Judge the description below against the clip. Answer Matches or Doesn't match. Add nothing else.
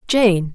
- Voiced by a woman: Matches